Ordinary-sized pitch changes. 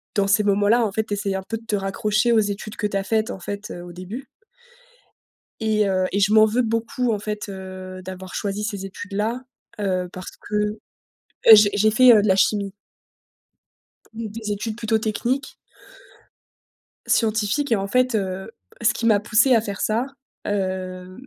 No: narrow, 2.2 semitones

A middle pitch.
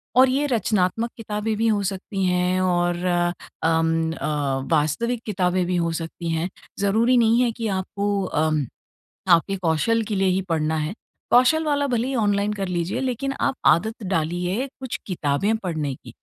No: high, 195 Hz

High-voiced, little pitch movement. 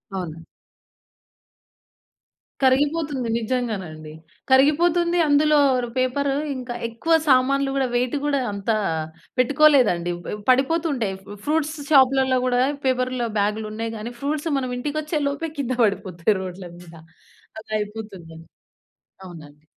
No: very high, 255 Hz; wide, 5.4 semitones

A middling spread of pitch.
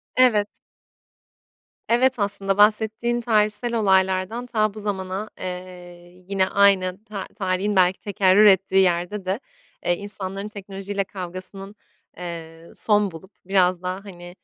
No: narrow, 2.2 semitones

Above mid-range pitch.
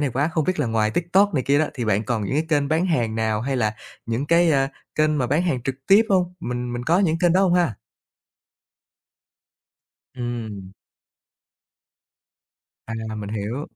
No: low, 135 Hz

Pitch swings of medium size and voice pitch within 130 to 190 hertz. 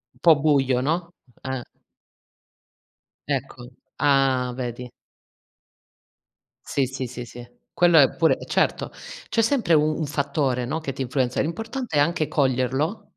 Yes: average, 4.0 semitones; medium, 140 Hz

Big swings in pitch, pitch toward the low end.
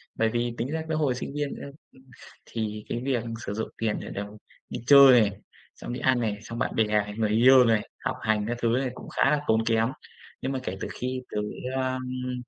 No: average, 2.8 semitones; low, 120 Hz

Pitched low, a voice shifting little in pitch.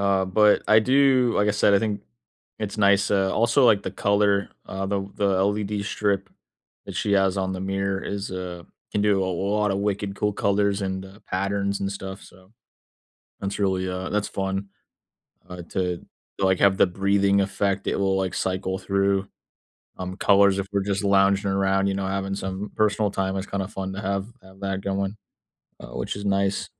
Yes: low, 100 Hz; narrow, 1.0 semitones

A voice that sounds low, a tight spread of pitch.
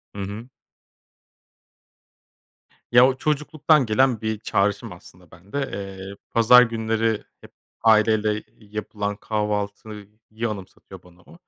Yes: low, 110 Hz; narrow, 2.2 semitones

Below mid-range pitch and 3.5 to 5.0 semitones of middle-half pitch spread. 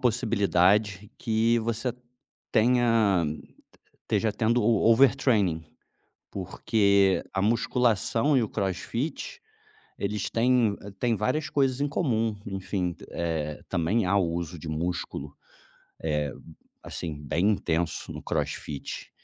Yes: low, 105 Hz; average, 4.7 semitones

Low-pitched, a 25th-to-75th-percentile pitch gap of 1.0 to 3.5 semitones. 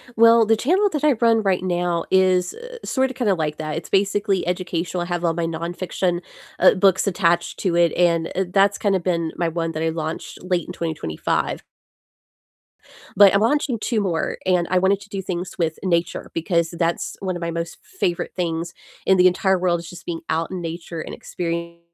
No: medium, 180 Hz; average, 2.7 semitones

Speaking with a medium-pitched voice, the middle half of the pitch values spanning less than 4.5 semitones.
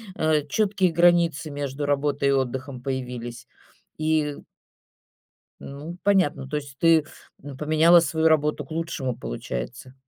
Yes: medium, 145 Hz; average, 3.2 semitones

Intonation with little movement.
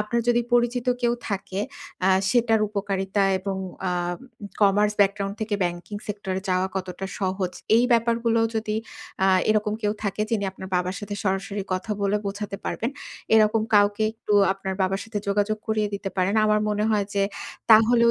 Yes: narrow, 2.0 semitones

